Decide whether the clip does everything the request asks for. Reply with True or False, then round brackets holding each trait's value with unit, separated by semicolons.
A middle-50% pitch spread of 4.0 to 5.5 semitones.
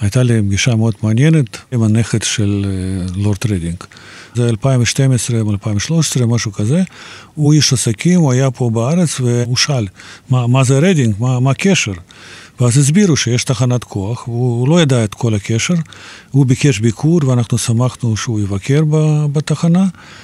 True (4.3 semitones)